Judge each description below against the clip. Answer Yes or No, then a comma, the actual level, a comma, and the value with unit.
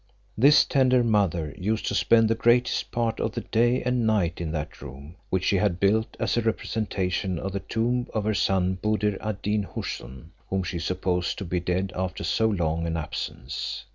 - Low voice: Yes, low, 100 Hz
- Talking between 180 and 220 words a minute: Yes, average, 195 wpm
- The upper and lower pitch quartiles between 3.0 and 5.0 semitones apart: Yes, average, 3.9 semitones